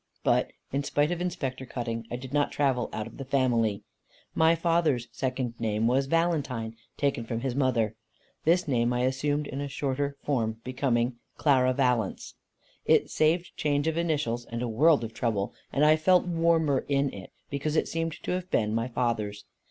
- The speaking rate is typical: Yes, average, 180 wpm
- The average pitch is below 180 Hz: Yes, low, 135 Hz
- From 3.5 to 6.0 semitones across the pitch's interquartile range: Yes, average, 4.4 semitones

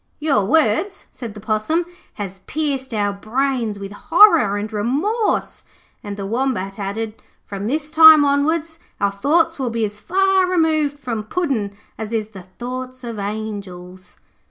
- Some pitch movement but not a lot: No, wide, 7.1 semitones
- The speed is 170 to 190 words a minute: No, average, 150 wpm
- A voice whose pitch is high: Yes, high, 235 Hz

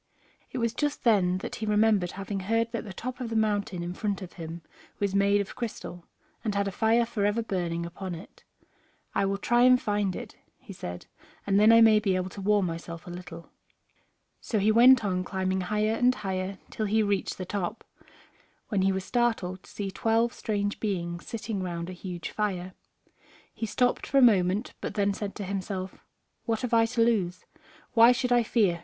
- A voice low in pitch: No, high, 205 Hz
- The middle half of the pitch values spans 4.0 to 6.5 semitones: No, average, 3.4 semitones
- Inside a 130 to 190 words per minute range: No, average, 200 wpm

